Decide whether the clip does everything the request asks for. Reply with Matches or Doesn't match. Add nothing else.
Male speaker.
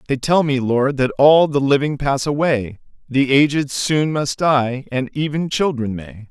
Matches